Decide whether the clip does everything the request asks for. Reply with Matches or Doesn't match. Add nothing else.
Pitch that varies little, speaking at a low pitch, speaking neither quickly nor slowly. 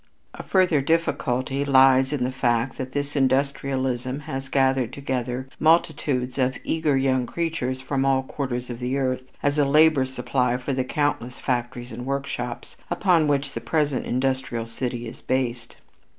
Matches